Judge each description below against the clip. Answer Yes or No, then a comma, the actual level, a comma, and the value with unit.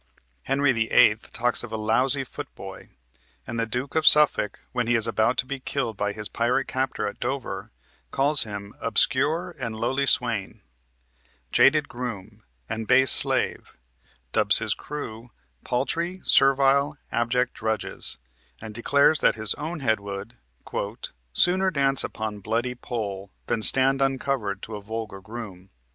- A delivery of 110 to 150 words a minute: Yes, average, 145 wpm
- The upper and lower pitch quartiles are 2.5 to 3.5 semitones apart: No, average, 3.9 semitones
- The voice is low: Yes, low, 120 Hz